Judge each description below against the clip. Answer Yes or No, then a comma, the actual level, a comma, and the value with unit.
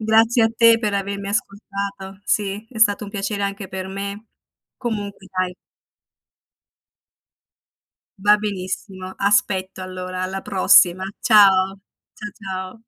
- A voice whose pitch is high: Yes, high, 200 Hz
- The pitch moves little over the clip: Yes, narrow, 1.8 semitones